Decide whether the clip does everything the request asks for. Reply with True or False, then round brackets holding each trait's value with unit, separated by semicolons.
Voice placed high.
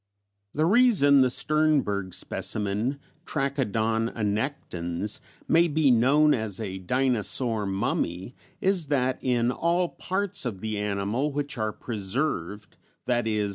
False (120 Hz)